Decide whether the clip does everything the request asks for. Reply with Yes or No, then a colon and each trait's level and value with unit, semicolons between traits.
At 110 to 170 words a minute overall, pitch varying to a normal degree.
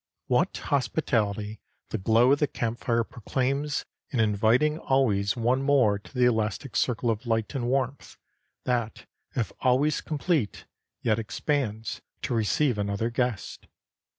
Yes: slow, 135 wpm; average, 3.7 semitones